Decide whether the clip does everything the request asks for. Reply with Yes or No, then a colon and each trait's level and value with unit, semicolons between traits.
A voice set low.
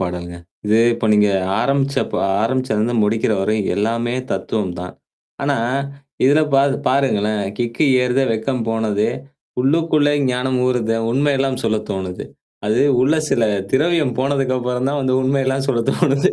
Yes: low, 125 Hz